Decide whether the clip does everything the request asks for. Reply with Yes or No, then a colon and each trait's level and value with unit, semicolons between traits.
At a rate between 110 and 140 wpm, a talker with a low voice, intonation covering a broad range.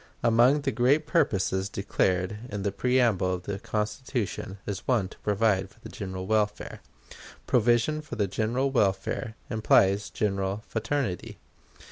No: slow, 135 wpm; low, 105 Hz; average, 3.6 semitones